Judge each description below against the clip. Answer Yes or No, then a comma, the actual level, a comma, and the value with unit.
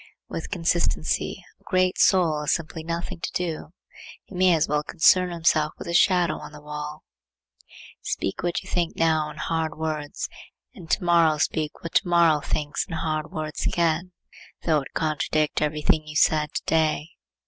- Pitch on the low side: No, medium, 160 Hz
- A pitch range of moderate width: No, narrow, 2.1 semitones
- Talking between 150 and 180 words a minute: Yes, average, 175 wpm